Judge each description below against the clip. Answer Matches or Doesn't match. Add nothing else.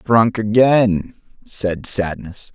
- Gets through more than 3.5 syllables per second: Doesn't match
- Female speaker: Doesn't match